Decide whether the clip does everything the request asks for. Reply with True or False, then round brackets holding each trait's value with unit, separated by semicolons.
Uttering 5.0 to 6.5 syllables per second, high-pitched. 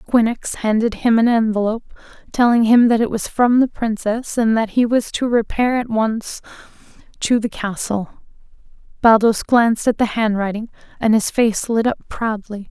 False (4.8 syllables/s; 225 Hz)